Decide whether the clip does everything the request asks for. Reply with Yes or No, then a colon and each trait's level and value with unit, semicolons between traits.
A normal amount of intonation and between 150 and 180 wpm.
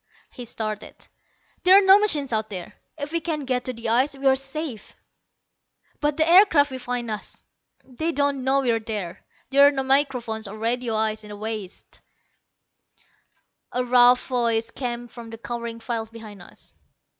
Yes: average, 3.9 semitones; average, 170 wpm